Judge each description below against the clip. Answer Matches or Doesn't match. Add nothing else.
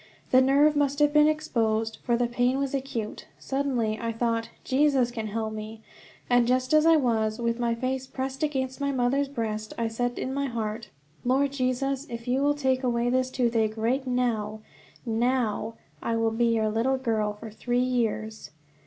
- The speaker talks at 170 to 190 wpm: Matches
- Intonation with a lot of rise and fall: Doesn't match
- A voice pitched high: Matches